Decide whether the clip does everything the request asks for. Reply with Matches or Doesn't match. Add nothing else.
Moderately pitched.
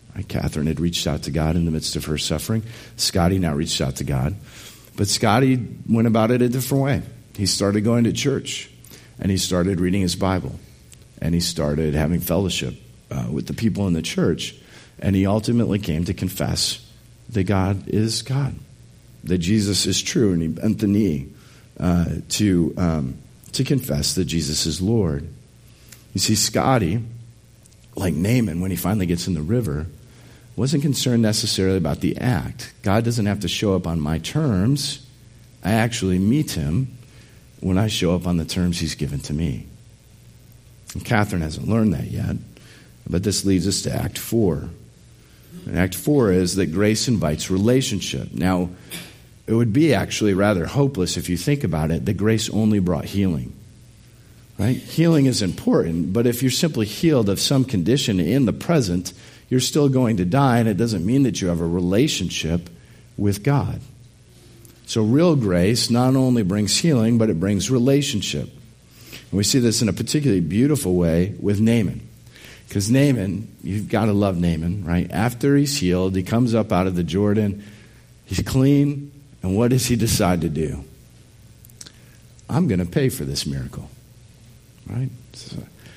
Doesn't match